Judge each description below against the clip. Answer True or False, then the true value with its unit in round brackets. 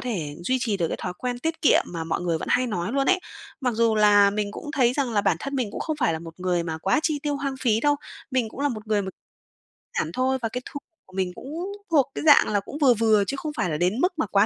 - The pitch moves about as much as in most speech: False (6.2 semitones)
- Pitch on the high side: True (225 Hz)